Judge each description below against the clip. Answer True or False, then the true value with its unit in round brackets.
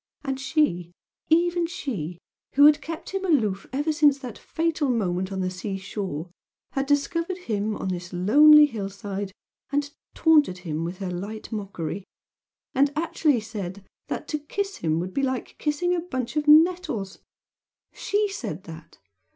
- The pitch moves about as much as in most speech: False (8.1 semitones)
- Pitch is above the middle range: True (250 Hz)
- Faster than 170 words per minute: False (160 wpm)